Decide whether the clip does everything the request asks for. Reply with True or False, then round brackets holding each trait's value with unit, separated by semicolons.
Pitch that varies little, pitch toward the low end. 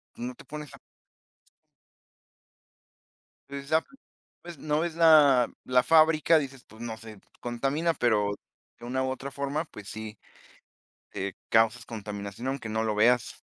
False (5.2 semitones; 125 Hz)